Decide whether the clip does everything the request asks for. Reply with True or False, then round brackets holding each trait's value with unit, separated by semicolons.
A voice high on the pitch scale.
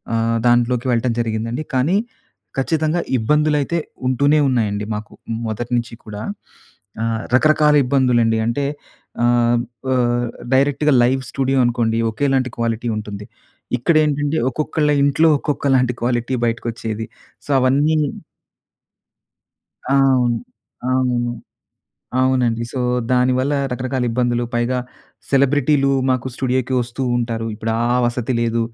False (125 Hz)